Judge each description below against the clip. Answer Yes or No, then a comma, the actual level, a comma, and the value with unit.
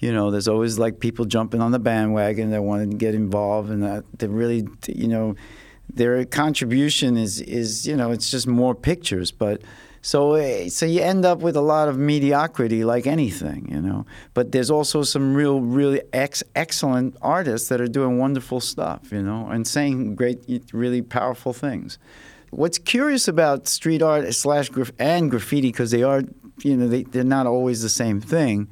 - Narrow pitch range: No, average, 4.2 semitones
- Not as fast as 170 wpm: No, average, 185 wpm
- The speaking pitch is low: Yes, low, 125 Hz